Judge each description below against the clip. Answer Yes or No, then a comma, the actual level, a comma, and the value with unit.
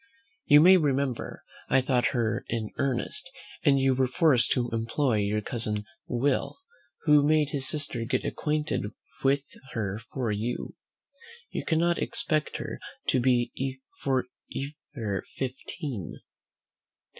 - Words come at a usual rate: No, slow, 125 wpm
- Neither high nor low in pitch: No, low, 130 Hz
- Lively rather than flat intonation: No, average, 3.8 semitones